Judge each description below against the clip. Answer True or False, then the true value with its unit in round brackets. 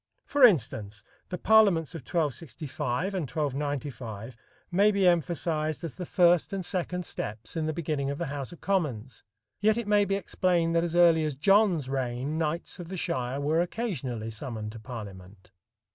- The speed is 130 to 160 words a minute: False (170 wpm)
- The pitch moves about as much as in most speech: False (5.8 semitones)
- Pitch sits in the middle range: True (155 Hz)